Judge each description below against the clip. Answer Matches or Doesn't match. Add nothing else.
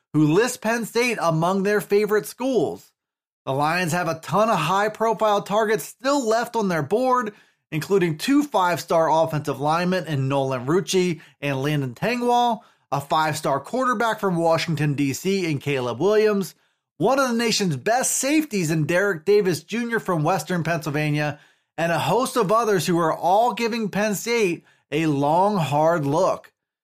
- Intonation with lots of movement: Matches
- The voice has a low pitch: Doesn't match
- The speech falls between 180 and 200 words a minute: Doesn't match